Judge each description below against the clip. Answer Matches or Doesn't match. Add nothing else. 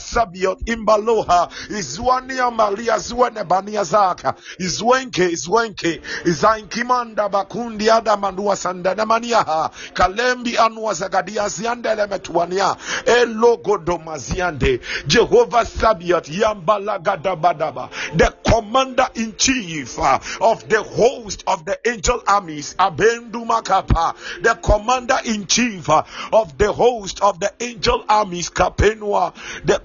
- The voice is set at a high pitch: Matches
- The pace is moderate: Doesn't match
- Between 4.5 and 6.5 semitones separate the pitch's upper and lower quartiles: Doesn't match